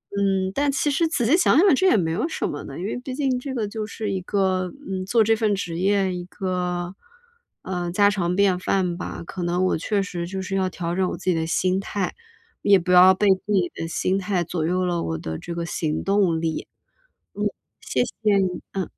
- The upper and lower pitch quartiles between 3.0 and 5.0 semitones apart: No, narrow, 2.6 semitones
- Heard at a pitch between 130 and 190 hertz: Yes, medium, 185 Hz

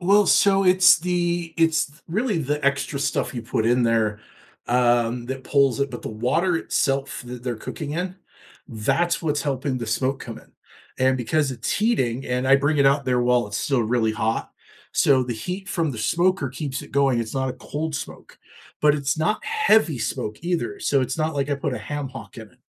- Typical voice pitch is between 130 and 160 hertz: Yes, medium, 140 Hz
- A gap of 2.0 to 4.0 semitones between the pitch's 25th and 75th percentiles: No, average, 4.8 semitones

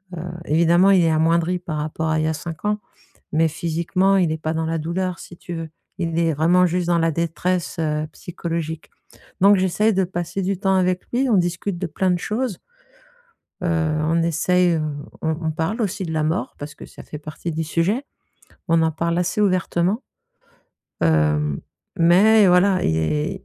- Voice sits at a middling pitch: Yes, medium, 170 Hz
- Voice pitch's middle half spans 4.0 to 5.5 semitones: No, narrow, 2.4 semitones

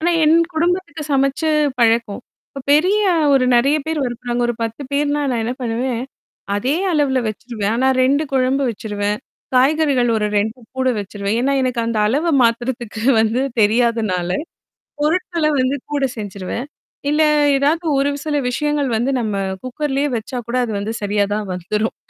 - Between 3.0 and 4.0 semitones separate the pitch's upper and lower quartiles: No, average, 4.5 semitones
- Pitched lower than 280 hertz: Yes, very high, 250 Hz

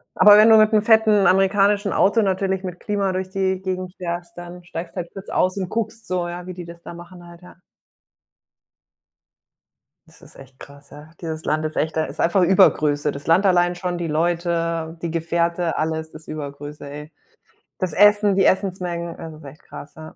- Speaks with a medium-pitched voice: Yes, medium, 175 Hz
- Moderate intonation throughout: Yes, average, 3.0 semitones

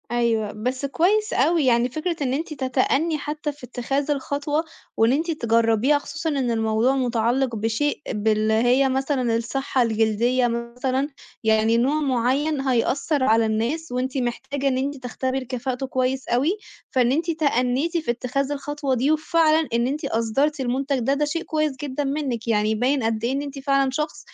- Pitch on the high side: Yes, very high, 265 Hz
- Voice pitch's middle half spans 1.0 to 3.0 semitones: No, average, 3.5 semitones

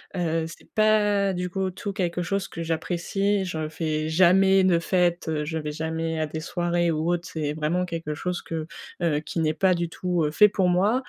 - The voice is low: No, medium, 175 Hz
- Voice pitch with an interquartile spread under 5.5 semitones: Yes, average, 2.7 semitones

